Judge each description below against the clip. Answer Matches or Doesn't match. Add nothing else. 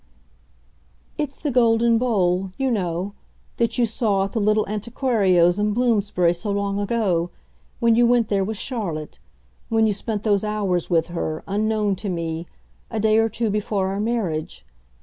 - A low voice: Doesn't match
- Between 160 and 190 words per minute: Matches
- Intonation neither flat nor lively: Matches